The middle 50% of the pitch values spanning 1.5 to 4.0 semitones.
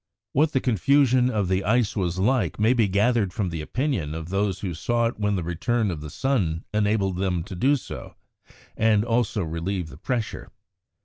No: average, 5.1 semitones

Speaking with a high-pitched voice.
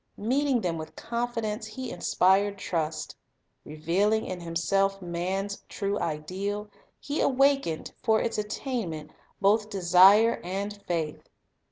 Yes: high, 200 Hz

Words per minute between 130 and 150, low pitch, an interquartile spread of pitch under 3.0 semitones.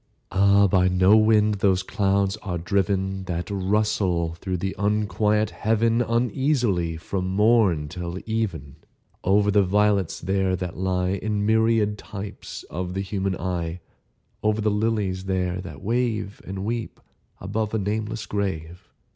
Yes: average, 140 wpm; low, 100 Hz; narrow, 2.5 semitones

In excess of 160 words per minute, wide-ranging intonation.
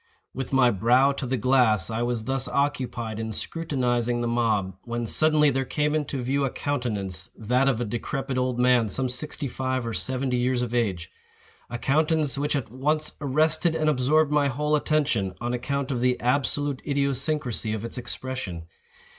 No: average, 170 wpm; average, 3.1 semitones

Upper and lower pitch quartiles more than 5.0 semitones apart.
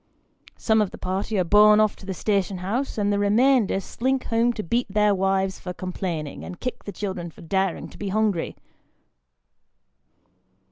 No: narrow, 2.5 semitones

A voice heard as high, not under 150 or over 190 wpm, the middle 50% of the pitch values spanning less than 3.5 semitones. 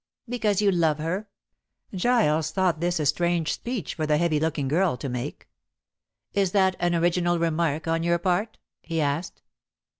No: medium, 170 Hz; average, 160 wpm; average, 3.0 semitones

